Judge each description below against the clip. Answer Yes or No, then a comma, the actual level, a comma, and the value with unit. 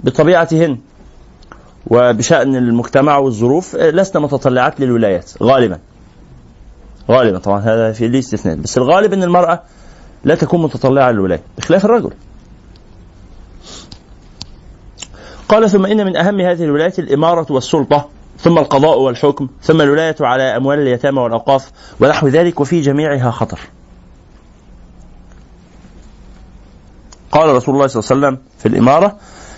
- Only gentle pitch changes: No, wide, 5.6 semitones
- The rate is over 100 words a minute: Yes, average, 110 wpm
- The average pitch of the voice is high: No, medium, 140 Hz